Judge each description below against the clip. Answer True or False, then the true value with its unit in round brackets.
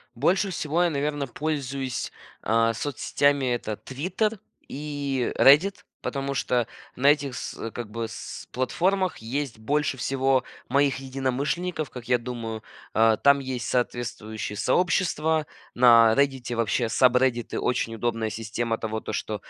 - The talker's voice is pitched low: True (130 Hz)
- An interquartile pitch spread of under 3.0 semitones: False (3.8 semitones)